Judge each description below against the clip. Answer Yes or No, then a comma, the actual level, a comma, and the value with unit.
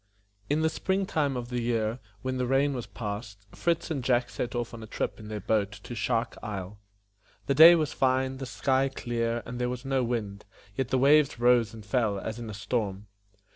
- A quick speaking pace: Yes, fast, 215 wpm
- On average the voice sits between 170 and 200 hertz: No, low, 120 Hz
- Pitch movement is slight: No, average, 3.3 semitones